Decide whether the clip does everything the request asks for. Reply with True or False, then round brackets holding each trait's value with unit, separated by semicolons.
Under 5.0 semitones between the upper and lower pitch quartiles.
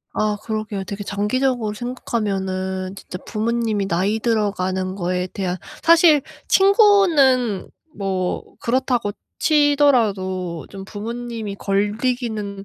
True (4.2 semitones)